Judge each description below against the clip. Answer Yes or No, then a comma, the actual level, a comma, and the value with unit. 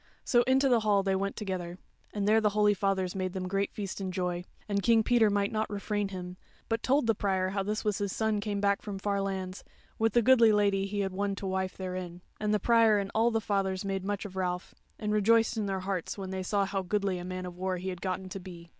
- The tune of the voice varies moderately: No, narrow, 2.1 semitones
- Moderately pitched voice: No, high, 200 Hz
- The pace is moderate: No, fast, 250 wpm